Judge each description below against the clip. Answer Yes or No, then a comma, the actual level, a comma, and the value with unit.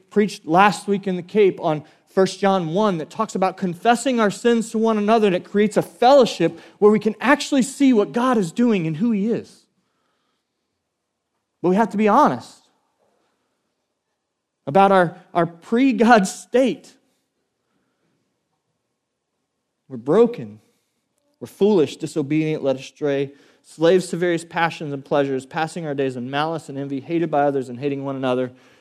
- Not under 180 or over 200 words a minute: No, average, 160 wpm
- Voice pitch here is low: No, medium, 185 Hz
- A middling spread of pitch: No, wide, 6.1 semitones